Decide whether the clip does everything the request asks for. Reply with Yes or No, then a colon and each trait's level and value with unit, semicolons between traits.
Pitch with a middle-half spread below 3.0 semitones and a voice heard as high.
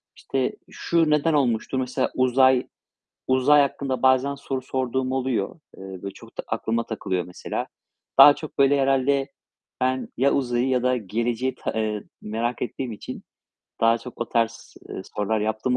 No: narrow, 2.6 semitones; low, 130 Hz